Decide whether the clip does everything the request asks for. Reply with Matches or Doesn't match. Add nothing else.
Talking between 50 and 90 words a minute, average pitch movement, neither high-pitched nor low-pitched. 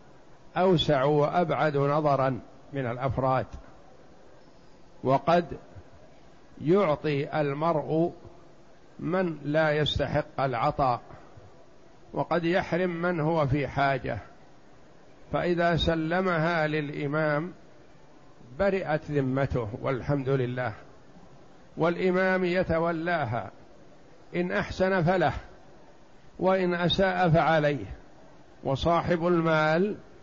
Matches